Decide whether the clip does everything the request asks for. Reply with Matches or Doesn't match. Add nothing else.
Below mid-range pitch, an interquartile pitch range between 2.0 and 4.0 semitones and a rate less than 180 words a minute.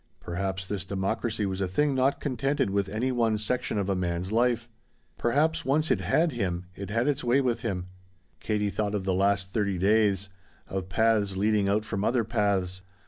Doesn't match